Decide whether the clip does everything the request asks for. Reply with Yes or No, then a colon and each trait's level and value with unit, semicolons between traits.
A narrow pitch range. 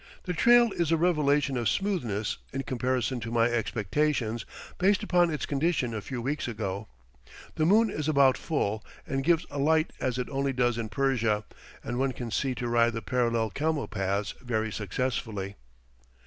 No: average, 4.9 semitones